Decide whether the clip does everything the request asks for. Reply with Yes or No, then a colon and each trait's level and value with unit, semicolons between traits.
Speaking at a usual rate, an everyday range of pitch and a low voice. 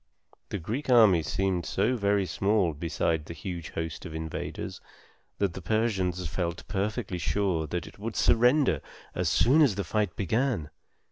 Yes: average, 155 wpm; average, 4.5 semitones; very low, 95 Hz